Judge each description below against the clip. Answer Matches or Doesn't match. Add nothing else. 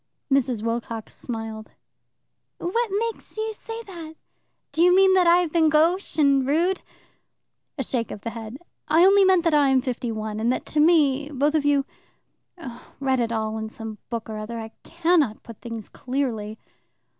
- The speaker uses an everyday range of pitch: Doesn't match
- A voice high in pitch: Matches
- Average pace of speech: Matches